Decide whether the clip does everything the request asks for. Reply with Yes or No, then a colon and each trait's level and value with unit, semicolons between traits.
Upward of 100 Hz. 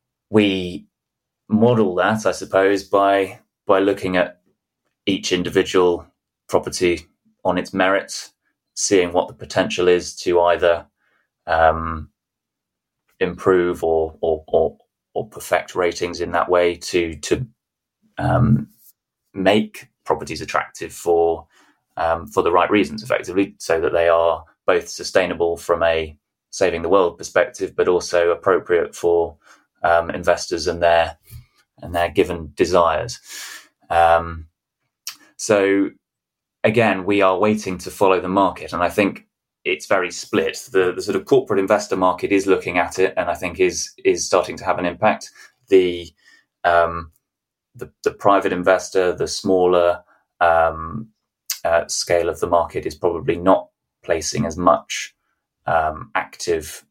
No: very low, 90 Hz